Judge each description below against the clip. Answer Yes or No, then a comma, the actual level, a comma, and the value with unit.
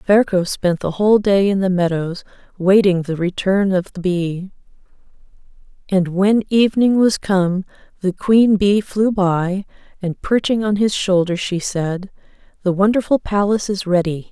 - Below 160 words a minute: Yes, average, 150 wpm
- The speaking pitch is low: No, high, 190 Hz